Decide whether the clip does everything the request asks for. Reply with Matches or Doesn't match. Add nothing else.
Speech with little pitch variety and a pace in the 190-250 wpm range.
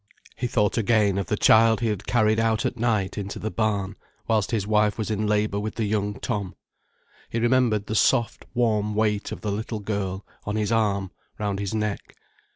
Matches